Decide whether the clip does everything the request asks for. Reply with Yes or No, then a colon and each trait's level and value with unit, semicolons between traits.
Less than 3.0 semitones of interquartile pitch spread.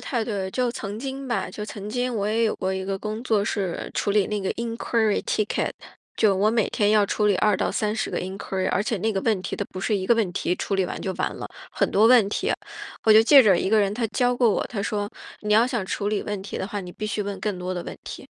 Yes: narrow, 2.4 semitones